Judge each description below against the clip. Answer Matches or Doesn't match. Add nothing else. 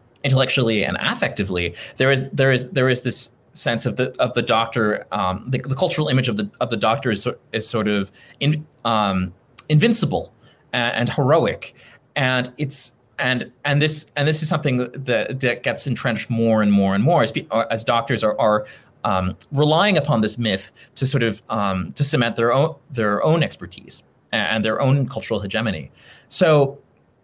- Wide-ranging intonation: Doesn't match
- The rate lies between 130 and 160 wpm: Doesn't match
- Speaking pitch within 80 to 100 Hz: Doesn't match